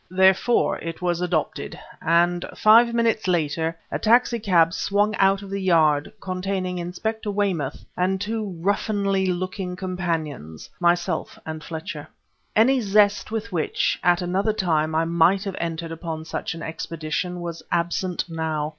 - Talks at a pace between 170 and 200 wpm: No, average, 145 wpm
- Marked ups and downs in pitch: No, average, 3.3 semitones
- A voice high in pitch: No, medium, 180 Hz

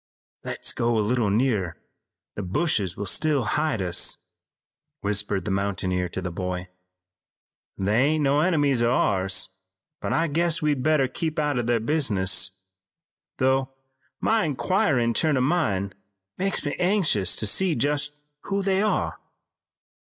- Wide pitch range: Yes, wide, 7.5 semitones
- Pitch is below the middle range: Yes, low, 125 Hz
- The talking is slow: No, average, 145 wpm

